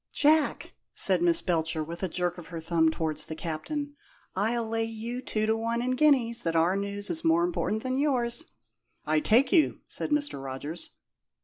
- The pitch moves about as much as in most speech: No, wide, 7.5 semitones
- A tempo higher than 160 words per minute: Yes, average, 185 wpm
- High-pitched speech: Yes, high, 215 Hz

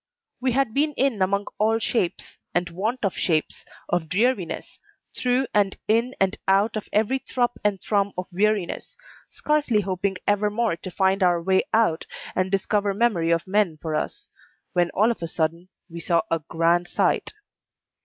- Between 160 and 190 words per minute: Yes, average, 170 wpm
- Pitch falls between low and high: No, high, 200 Hz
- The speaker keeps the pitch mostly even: No, average, 4.2 semitones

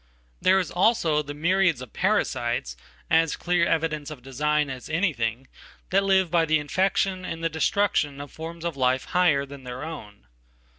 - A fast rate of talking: No, average, 160 wpm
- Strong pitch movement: No, average, 4.1 semitones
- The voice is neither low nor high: Yes, medium, 155 Hz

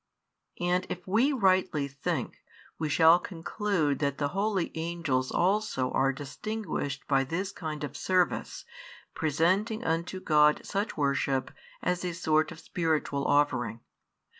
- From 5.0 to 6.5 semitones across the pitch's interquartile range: No, average, 4.6 semitones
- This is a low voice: No, medium, 160 Hz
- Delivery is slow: Yes, slow, 130 wpm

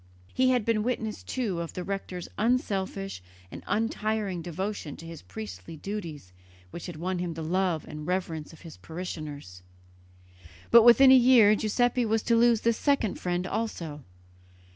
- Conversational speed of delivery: Yes, average, 160 wpm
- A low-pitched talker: No, high, 190 Hz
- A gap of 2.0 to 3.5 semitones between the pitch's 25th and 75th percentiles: No, wide, 5.4 semitones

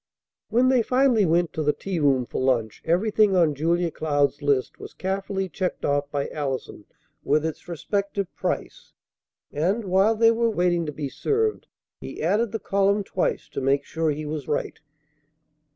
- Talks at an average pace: Yes, average, 170 wpm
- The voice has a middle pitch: Yes, medium, 175 Hz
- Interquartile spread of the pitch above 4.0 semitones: Yes, wide, 5.5 semitones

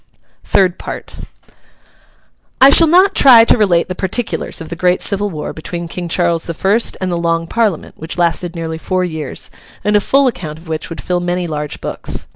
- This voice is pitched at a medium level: Yes, medium, 175 Hz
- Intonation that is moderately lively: Yes, average, 3.7 semitones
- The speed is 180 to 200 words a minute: Yes, average, 195 wpm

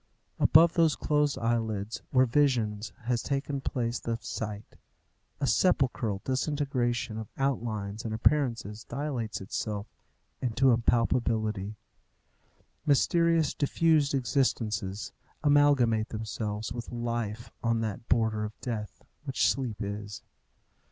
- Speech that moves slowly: Yes, slow, 110 wpm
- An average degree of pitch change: Yes, average, 4.1 semitones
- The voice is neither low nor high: No, low, 115 Hz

